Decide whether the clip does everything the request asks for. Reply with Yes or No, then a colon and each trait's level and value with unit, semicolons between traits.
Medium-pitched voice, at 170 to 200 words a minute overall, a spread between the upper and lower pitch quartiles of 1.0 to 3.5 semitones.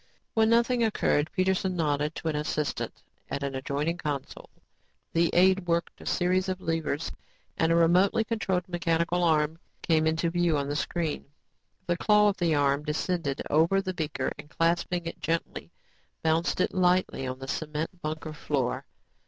No: medium, 165 Hz; average, 160 wpm; average, 3.1 semitones